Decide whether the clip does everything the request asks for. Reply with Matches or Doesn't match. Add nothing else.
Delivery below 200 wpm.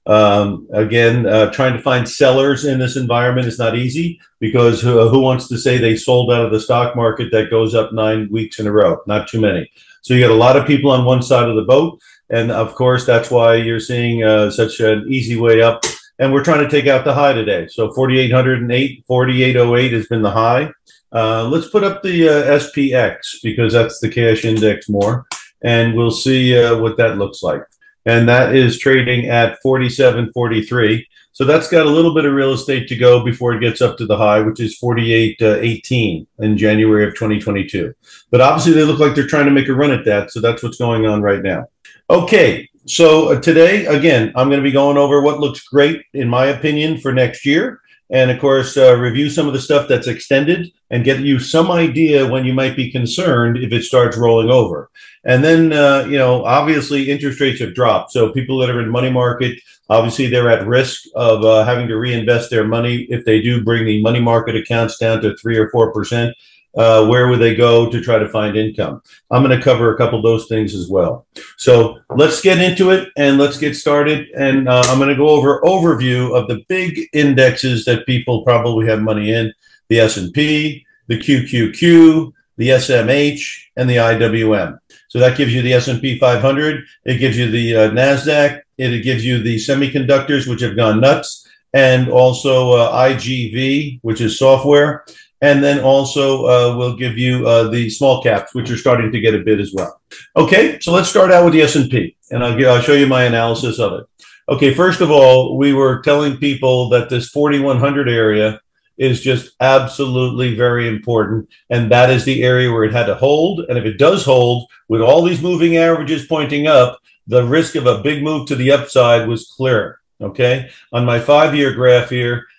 Doesn't match